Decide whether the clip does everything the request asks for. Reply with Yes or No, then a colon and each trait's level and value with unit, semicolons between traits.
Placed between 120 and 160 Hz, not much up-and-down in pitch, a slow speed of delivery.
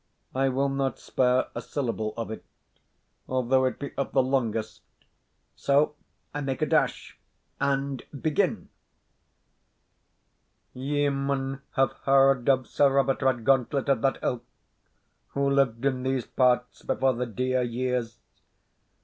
Yes: low, 135 Hz; narrow, 1.6 semitones; slow, 130 wpm